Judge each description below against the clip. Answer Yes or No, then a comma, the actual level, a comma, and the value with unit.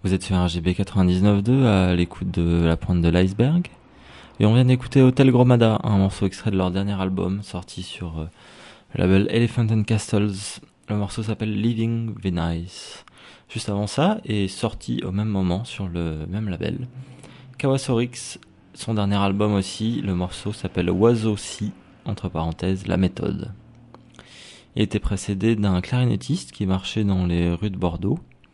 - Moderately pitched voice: No, low, 100 Hz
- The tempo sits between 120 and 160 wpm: Yes, average, 155 wpm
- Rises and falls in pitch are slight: No, average, 3.9 semitones